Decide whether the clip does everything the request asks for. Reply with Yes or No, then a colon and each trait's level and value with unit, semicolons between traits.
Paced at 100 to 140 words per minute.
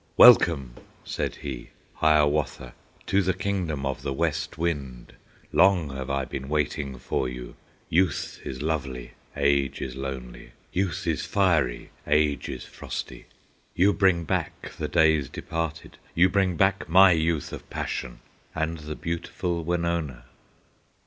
Yes: slow, 135 wpm